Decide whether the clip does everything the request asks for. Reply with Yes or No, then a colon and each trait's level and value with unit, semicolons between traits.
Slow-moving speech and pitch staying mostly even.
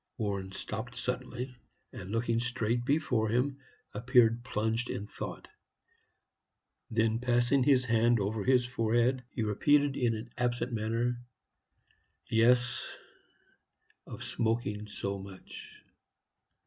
Yes: slow, 110 wpm; narrow, 2.1 semitones